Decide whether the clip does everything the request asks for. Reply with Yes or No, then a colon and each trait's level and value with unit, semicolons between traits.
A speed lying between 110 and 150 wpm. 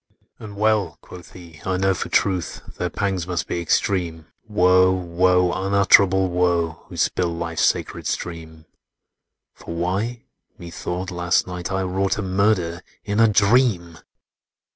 Yes: average, 140 wpm